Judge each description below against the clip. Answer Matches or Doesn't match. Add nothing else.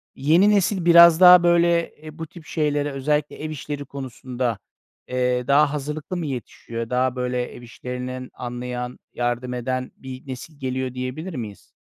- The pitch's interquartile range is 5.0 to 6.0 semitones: Doesn't match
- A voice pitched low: Matches